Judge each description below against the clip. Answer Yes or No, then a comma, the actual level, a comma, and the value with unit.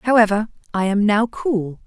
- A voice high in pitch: Yes, high, 210 Hz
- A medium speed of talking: Yes, average, 160 wpm